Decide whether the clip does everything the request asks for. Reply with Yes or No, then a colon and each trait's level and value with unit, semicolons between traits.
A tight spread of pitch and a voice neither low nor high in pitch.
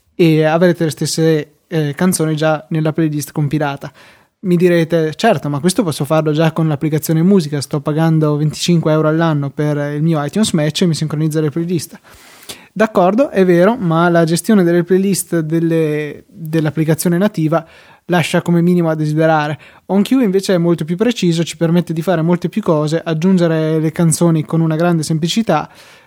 Yes: narrow, 2.1 semitones; medium, 165 Hz